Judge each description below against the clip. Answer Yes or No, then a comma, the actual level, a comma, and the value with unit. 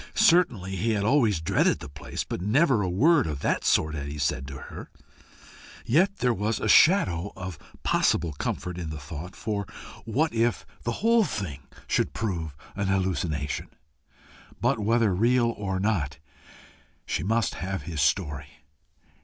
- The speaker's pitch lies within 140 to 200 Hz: No, very low, 95 Hz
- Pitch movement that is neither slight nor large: No, wide, 6.9 semitones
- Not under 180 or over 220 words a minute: No, average, 155 wpm